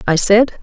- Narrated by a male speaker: No, female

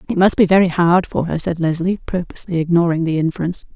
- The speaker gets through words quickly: Yes, fast, 210 wpm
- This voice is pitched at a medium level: Yes, medium, 175 Hz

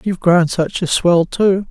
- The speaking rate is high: Yes, fast, 210 wpm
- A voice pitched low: No, medium, 180 Hz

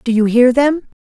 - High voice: Yes, very high, 250 Hz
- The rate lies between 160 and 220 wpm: No, fast, 235 wpm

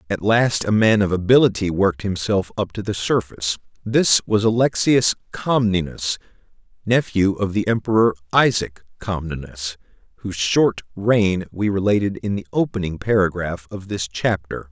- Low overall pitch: Yes, low, 100 Hz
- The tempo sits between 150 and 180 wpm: No, average, 140 wpm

